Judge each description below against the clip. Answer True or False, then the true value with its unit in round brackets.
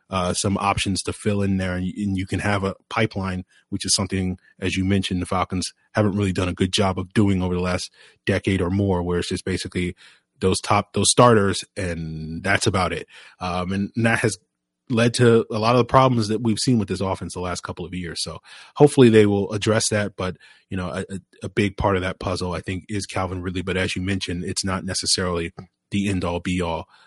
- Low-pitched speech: True (95 Hz)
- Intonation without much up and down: True (2.1 semitones)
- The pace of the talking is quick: True (230 wpm)